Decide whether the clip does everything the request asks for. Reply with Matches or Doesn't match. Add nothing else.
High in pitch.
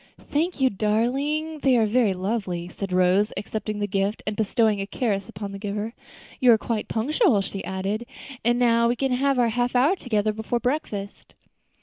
Matches